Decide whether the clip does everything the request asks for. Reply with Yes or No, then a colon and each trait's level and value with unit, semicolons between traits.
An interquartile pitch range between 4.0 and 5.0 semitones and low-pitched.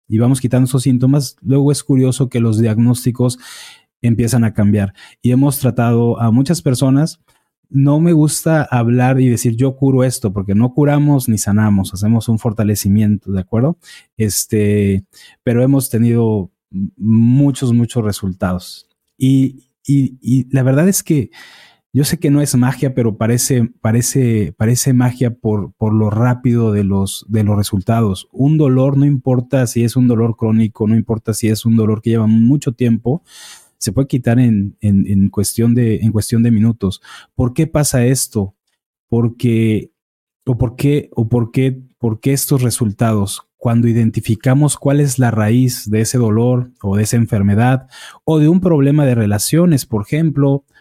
No: average, 3.3 semitones; low, 120 Hz